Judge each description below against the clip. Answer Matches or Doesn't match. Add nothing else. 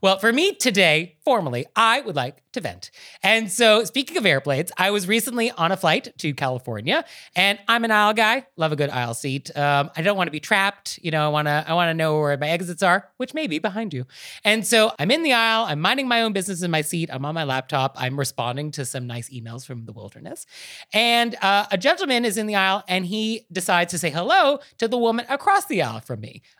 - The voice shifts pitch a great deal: Matches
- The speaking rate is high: Matches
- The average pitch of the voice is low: Doesn't match